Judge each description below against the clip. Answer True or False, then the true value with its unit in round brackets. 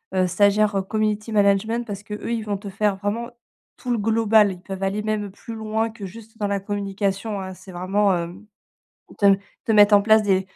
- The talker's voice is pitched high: True (205 Hz)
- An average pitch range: False (1.7 semitones)